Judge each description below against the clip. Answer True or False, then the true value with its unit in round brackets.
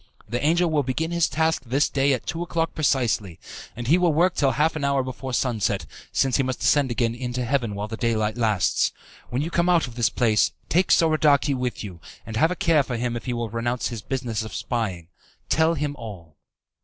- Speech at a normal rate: False (215 wpm)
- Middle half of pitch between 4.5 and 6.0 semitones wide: True (4.9 semitones)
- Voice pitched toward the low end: True (130 Hz)